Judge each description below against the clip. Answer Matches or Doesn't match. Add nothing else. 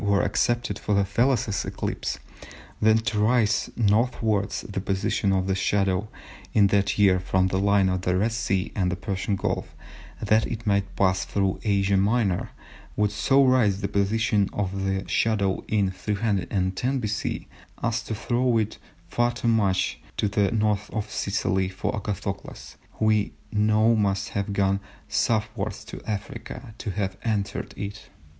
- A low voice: Matches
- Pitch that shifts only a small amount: Matches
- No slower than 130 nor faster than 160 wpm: Matches